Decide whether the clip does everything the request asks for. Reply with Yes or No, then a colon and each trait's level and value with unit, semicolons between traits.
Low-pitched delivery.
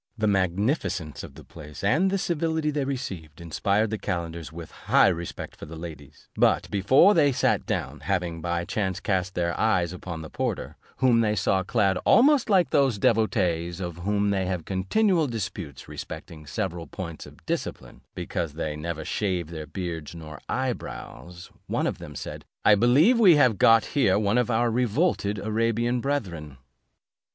Yes: low, 100 Hz